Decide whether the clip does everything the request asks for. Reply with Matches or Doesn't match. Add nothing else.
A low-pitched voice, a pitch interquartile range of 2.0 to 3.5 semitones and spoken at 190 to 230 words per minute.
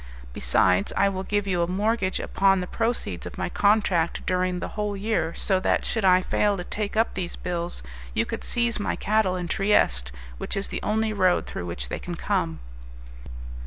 Doesn't match